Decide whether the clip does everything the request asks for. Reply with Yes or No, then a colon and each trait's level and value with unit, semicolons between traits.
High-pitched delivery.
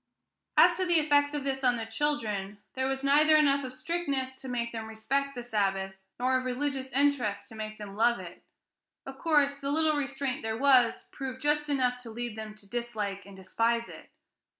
Yes: very high, 255 Hz